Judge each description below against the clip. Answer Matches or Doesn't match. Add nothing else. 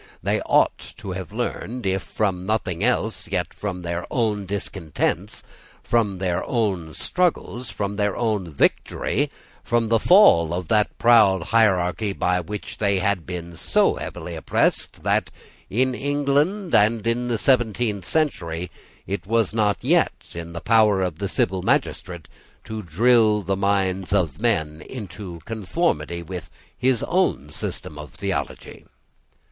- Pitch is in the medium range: Doesn't match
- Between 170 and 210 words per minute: Doesn't match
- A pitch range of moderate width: Matches